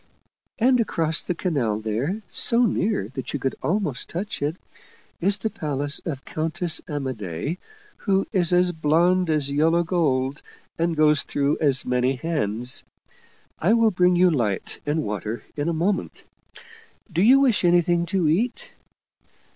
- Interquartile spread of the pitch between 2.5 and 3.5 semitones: No, average, 4.7 semitones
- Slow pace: No, average, 145 wpm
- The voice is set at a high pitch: No, medium, 160 Hz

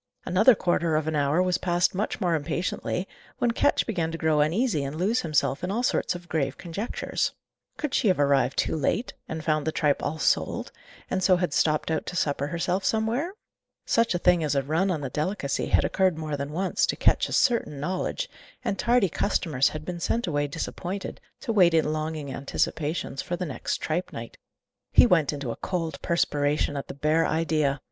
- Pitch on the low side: No, medium, 165 Hz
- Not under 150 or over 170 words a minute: No, average, 200 wpm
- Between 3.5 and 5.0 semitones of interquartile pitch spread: Yes, average, 3.8 semitones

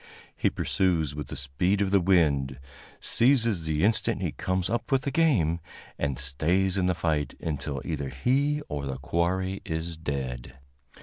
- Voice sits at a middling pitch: No, very low, 85 Hz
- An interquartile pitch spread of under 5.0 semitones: No, wide, 5.4 semitones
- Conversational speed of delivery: Yes, average, 165 wpm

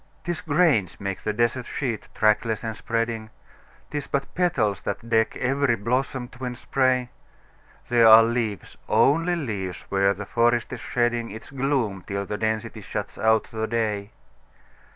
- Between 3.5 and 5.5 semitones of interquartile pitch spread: No, average, 3.0 semitones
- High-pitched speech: No, low, 115 Hz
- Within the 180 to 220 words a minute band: No, average, 150 wpm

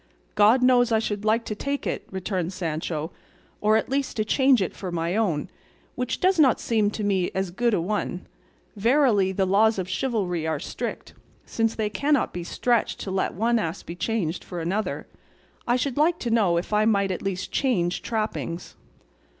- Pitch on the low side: No, high, 210 Hz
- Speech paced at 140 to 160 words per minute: No, average, 190 wpm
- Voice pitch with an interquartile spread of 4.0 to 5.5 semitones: Yes, average, 4.4 semitones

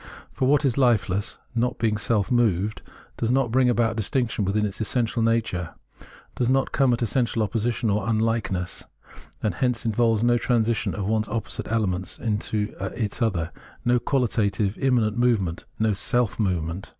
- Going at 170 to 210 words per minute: No, average, 155 wpm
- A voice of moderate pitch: No, low, 110 Hz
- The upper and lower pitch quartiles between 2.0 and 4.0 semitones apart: Yes, average, 2.9 semitones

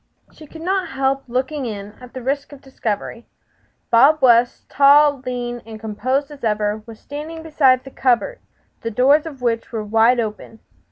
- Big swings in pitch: No, average, 3.9 semitones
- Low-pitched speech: No, very high, 255 Hz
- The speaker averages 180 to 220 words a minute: No, average, 170 wpm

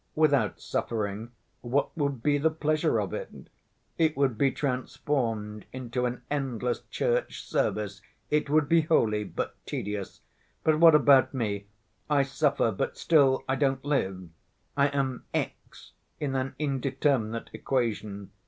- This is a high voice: No, low, 135 Hz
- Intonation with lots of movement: No, average, 4.5 semitones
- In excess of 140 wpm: No, slow, 135 wpm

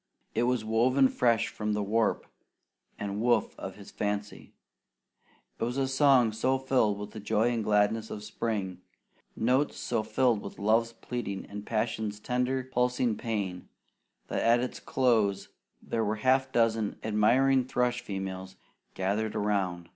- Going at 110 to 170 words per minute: Yes, average, 150 wpm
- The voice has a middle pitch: No, low, 110 Hz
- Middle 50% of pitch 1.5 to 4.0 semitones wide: Yes, average, 3.1 semitones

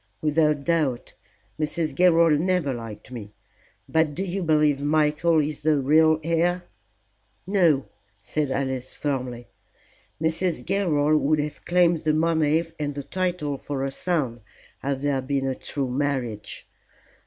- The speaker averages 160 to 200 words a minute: No, slow, 135 wpm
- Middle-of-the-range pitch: Yes, medium, 150 Hz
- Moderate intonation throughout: Yes, average, 3.2 semitones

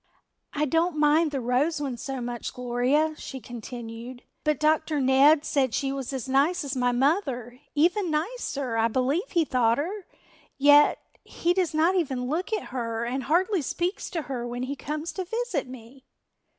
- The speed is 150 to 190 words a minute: Yes, average, 175 wpm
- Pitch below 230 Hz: No, very high, 280 Hz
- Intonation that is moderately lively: Yes, average, 4.5 semitones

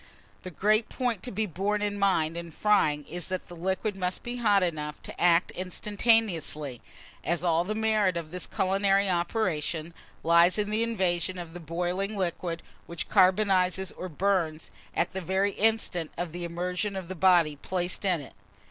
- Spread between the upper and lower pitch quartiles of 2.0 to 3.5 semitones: Yes, average, 3.0 semitones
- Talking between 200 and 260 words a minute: No, average, 175 wpm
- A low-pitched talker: No, medium, 185 Hz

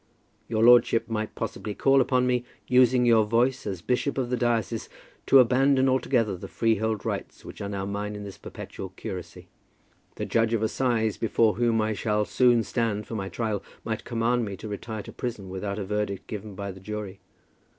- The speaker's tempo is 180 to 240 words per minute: Yes, average, 190 wpm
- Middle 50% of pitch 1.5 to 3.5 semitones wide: Yes, average, 2.9 semitones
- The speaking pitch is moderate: No, low, 110 Hz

